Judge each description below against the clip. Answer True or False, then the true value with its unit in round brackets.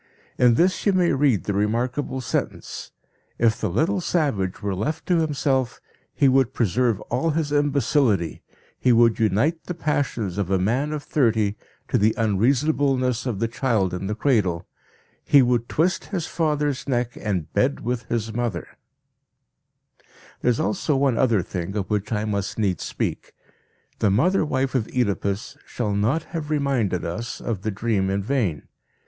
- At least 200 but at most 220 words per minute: False (165 wpm)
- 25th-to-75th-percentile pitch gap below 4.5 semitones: False (5.5 semitones)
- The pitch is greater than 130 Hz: False (120 Hz)